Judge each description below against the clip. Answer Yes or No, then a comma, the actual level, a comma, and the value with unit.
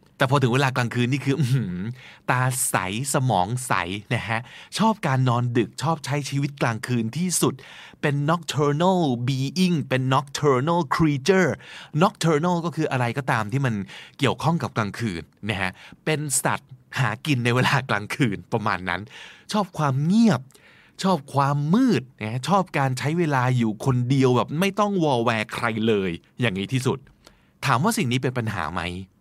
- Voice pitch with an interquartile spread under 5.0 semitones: Yes, average, 4.6 semitones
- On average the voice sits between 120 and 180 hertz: Yes, low, 135 Hz